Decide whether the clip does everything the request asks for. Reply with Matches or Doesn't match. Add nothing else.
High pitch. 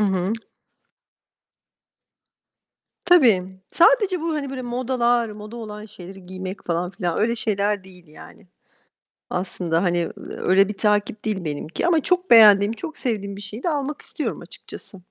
Matches